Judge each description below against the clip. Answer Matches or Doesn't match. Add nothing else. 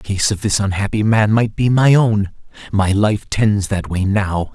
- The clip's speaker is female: Doesn't match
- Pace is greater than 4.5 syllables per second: Doesn't match